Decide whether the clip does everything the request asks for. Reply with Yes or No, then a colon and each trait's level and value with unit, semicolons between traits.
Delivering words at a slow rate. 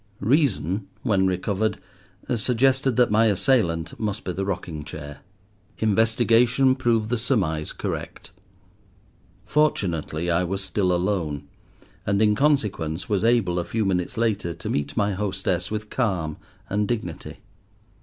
Yes: slow, 130 wpm